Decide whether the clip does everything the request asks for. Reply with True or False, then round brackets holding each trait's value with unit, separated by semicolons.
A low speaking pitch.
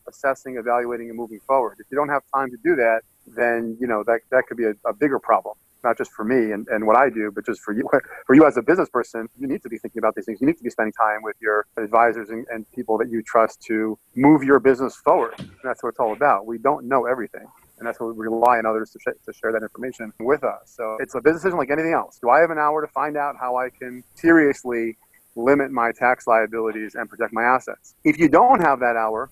True (120 Hz)